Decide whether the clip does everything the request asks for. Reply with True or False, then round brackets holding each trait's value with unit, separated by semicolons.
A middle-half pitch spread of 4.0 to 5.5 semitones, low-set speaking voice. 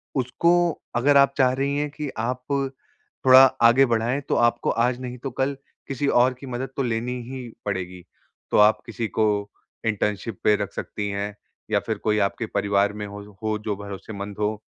True (4.3 semitones; 120 Hz)